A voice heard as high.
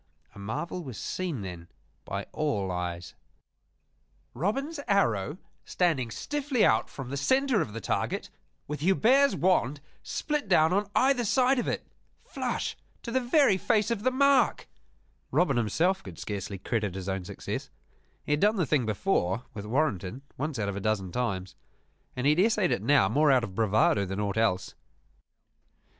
No: medium, 140 Hz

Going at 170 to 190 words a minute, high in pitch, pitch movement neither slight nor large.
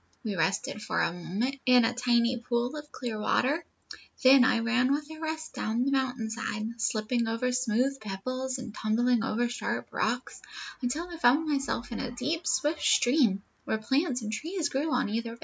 Yes: average, 185 wpm; high, 245 Hz; average, 3.2 semitones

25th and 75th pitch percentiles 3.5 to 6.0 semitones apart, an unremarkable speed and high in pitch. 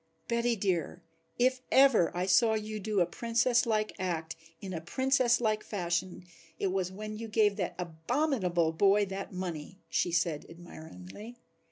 Yes: average, 4.7 semitones; average, 155 wpm; high, 195 Hz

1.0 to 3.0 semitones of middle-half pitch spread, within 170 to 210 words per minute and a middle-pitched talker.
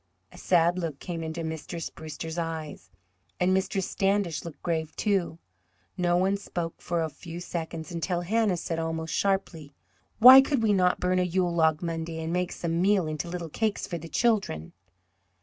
Yes: narrow, 2.5 semitones; average, 175 wpm; medium, 170 Hz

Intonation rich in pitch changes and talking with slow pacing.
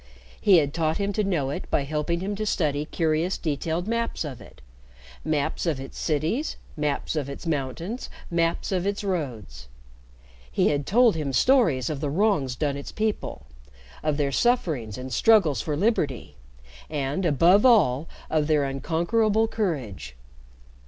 No: wide, 5.9 semitones; average, 155 wpm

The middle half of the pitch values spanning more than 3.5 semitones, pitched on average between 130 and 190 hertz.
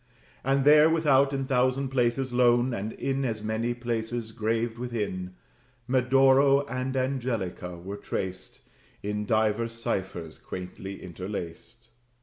No: average, 4.1 semitones; low, 120 Hz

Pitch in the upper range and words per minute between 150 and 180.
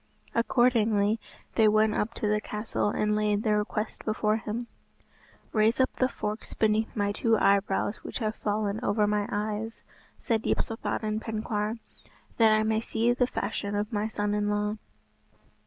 Yes: high, 215 Hz; average, 155 wpm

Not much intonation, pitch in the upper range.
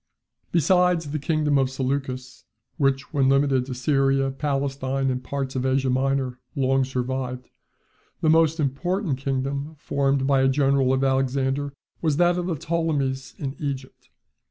No: narrow, 1.6 semitones; low, 135 Hz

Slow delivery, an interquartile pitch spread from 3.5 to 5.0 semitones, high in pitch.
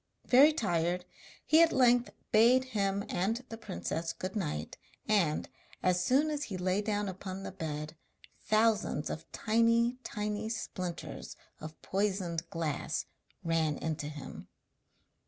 No: slow, 130 wpm; wide, 5.5 semitones; high, 195 Hz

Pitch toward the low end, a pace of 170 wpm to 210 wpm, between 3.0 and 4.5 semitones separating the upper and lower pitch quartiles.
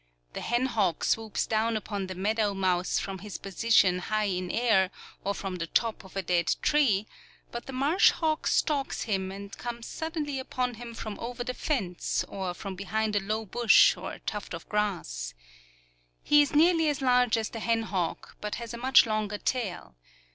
No: high, 215 Hz; average, 185 wpm; average, 4.2 semitones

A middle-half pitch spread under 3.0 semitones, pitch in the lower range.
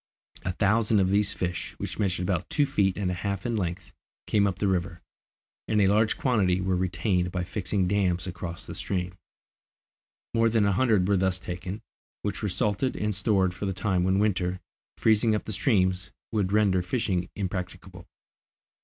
Yes: narrow, 2.4 semitones; very low, 95 Hz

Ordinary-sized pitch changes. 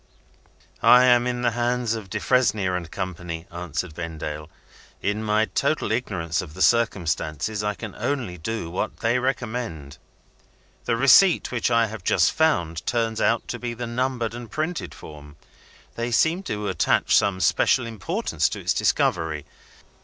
No: wide, 5.7 semitones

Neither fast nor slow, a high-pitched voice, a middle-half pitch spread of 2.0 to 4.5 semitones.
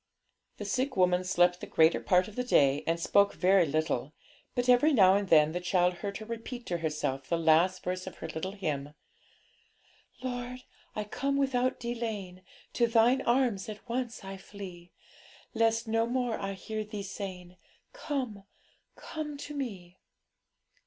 No: average, 160 wpm; high, 200 Hz; average, 5.2 semitones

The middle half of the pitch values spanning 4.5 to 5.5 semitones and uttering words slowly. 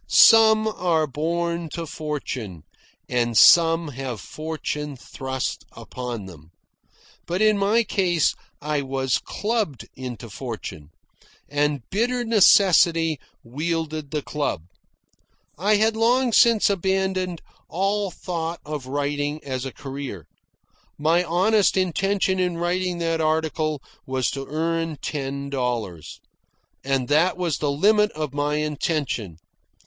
Yes: average, 5.1 semitones; slow, 120 wpm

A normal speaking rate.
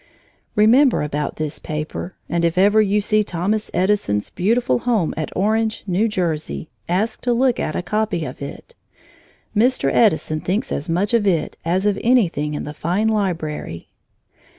Yes: average, 160 wpm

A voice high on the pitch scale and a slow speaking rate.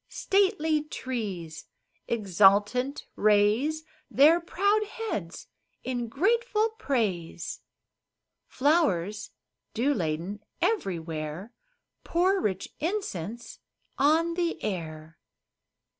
Yes: high, 240 Hz; slow, 75 wpm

